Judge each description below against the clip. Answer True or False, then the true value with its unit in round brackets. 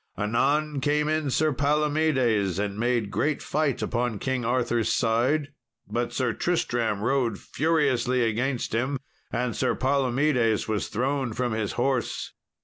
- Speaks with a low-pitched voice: True (125 Hz)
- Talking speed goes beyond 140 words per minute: False (135 wpm)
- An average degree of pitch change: True (3.8 semitones)